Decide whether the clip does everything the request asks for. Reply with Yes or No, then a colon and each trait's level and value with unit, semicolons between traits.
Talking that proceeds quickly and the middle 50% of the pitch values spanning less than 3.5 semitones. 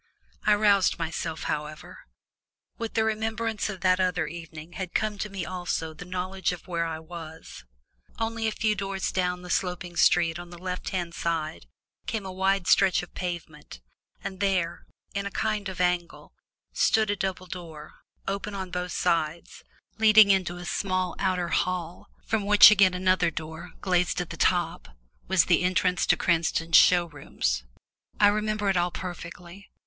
No: average, 165 wpm; narrow, 2.4 semitones